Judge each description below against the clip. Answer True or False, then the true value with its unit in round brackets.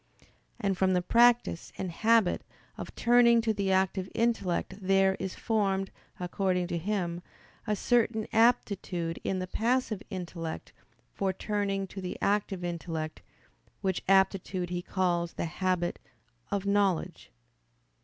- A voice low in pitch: False (190 Hz)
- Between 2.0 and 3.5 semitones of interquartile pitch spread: True (2.8 semitones)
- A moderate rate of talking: False (130 wpm)